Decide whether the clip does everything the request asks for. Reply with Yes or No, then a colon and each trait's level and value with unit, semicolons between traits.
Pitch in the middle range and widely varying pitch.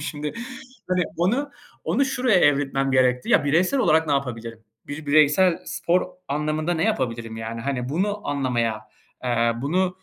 Yes: medium, 145 Hz; wide, 5.8 semitones